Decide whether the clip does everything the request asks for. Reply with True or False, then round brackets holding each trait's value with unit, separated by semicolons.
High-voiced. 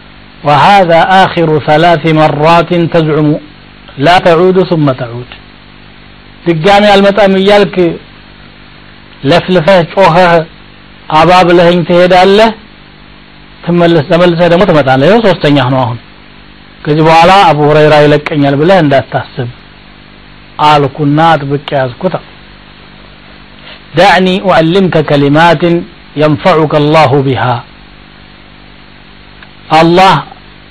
False (165 Hz)